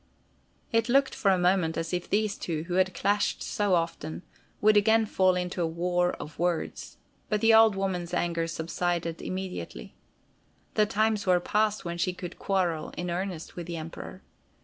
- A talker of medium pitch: Yes, medium, 180 Hz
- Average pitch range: Yes, average, 3.2 semitones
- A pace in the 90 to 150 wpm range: No, average, 170 wpm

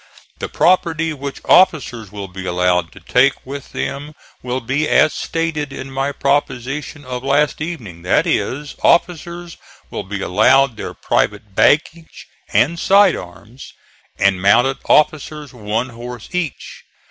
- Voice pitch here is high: No, low, 135 Hz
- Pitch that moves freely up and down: Yes, wide, 5.9 semitones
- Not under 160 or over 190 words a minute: No, slow, 135 wpm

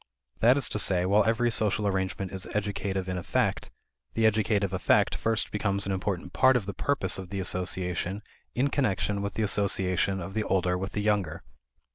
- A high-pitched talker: No, low, 100 Hz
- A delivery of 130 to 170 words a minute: No, average, 185 wpm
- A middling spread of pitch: No, narrow, 2.3 semitones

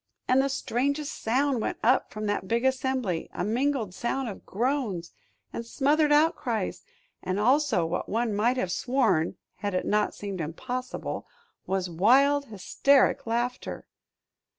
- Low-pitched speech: No, high, 240 Hz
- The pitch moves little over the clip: No, average, 4.8 semitones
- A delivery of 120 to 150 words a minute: Yes, average, 140 wpm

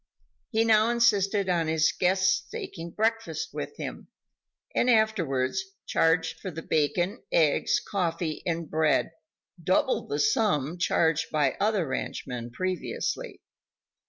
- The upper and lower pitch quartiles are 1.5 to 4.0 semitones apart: No, average, 5.1 semitones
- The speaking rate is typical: No, slow, 120 wpm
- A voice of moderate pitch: Yes, medium, 180 Hz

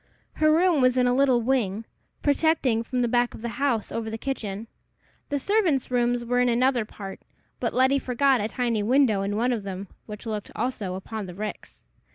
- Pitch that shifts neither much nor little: Yes, average, 3.5 semitones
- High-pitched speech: Yes, high, 240 Hz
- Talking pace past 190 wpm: Yes, average, 200 wpm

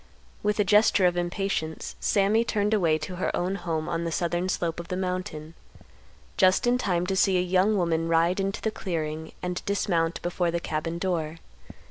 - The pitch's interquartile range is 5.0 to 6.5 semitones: No, average, 2.8 semitones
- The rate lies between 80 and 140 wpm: No, average, 185 wpm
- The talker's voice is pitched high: No, medium, 180 Hz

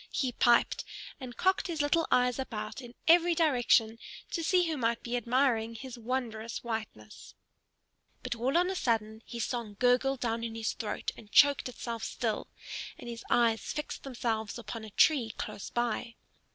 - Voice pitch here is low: No, high, 240 Hz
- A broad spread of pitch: No, average, 3.1 semitones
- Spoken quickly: No, average, 165 wpm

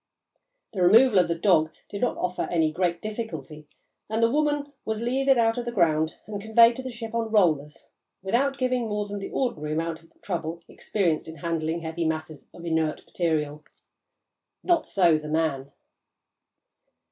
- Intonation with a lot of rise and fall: Yes, wide, 6.2 semitones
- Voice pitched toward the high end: No, medium, 180 Hz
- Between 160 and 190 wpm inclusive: Yes, average, 170 wpm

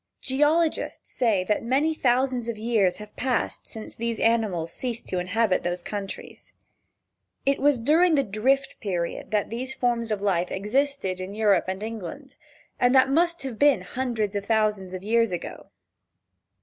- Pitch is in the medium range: No, high, 225 Hz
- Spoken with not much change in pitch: No, average, 4.8 semitones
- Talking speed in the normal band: Yes, average, 160 wpm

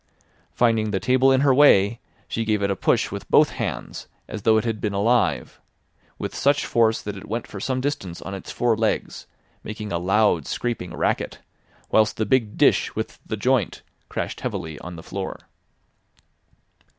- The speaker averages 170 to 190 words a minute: Yes, average, 175 wpm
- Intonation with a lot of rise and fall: No, average, 3.4 semitones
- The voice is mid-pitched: No, low, 110 Hz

